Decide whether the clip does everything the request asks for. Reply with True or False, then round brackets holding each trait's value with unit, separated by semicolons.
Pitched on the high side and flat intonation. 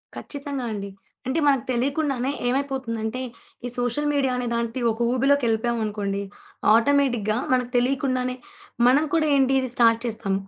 False (250 Hz; 3.1 semitones)